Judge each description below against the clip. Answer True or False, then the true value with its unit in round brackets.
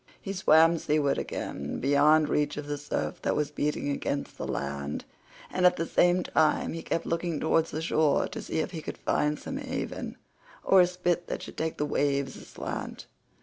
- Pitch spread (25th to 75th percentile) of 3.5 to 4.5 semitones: False (3.0 semitones)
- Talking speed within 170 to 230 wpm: True (190 wpm)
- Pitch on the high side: False (155 Hz)